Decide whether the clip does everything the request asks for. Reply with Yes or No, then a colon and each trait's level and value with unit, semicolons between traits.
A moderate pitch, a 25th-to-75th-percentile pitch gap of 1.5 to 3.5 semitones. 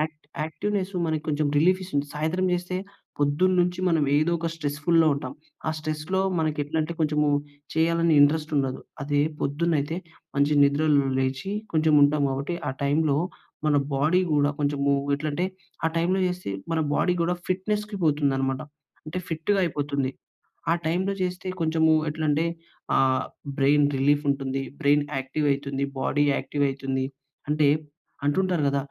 Yes: medium, 150 Hz; average, 2.9 semitones